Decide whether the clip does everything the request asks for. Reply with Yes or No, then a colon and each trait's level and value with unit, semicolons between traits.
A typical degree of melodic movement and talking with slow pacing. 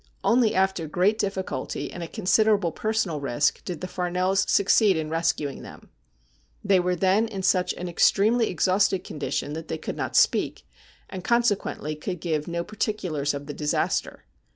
No: average, 3.9 semitones; average, 170 wpm